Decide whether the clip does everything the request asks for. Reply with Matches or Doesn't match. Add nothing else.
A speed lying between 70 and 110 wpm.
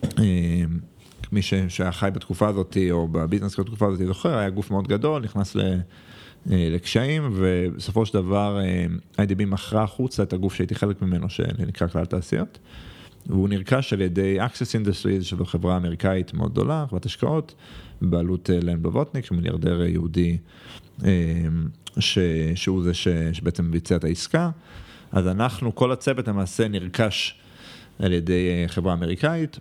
Doesn't match